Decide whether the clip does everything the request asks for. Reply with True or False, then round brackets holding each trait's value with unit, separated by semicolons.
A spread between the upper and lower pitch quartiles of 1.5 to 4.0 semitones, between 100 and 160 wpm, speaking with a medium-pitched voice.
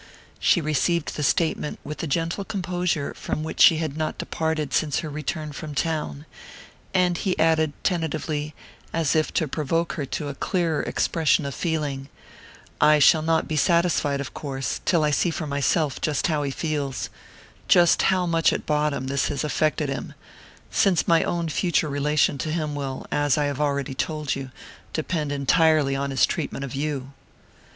False (2.5 semitones; 175 wpm; 155 Hz)